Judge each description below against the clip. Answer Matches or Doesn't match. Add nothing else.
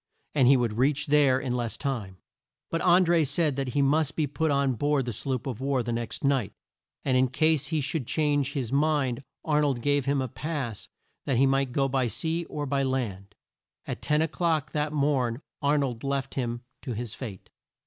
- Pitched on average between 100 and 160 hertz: Matches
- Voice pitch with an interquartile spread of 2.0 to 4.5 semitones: Matches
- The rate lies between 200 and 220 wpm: Matches